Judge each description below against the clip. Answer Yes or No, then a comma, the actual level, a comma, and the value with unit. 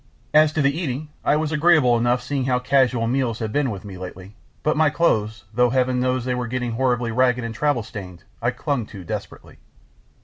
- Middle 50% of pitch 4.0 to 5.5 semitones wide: No, average, 3.4 semitones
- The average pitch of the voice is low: Yes, low, 125 Hz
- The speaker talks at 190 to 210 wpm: Yes, fast, 205 wpm